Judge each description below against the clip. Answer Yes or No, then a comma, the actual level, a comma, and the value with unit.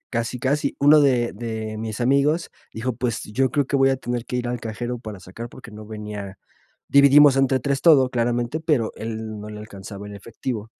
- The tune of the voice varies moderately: Yes, average, 3.6 semitones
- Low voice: Yes, low, 120 Hz